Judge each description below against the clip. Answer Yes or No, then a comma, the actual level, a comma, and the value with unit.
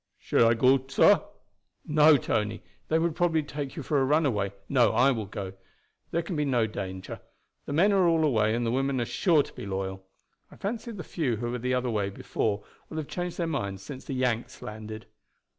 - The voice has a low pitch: Yes, low, 130 Hz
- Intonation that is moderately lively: No, wide, 6.1 semitones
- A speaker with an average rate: No, fast, 210 wpm